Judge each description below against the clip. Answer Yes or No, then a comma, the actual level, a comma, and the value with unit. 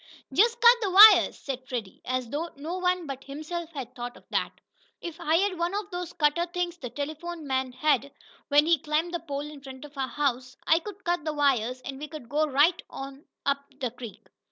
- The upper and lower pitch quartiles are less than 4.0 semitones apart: No, average, 4.3 semitones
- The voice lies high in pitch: Yes, very high, 295 Hz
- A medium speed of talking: No, fast, 215 wpm